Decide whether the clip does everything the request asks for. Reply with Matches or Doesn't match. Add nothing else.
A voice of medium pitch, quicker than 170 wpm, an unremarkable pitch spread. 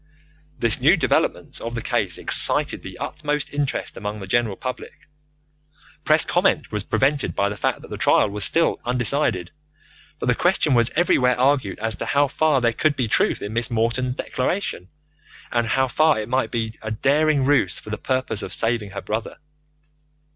Doesn't match